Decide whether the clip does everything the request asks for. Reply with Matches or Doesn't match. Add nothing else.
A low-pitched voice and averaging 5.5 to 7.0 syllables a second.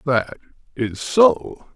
Doesn't match